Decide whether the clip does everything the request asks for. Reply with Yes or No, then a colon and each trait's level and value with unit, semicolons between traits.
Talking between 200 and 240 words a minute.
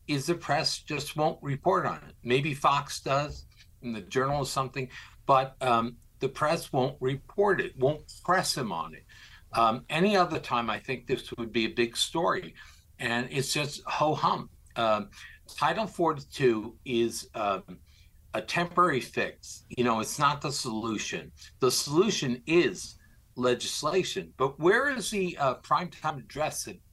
No: average, 160 wpm